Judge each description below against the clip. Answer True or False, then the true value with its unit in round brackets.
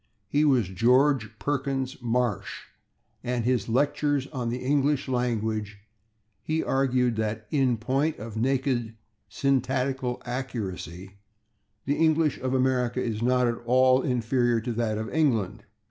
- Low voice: True (125 Hz)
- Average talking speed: False (130 wpm)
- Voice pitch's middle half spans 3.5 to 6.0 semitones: False (3.0 semitones)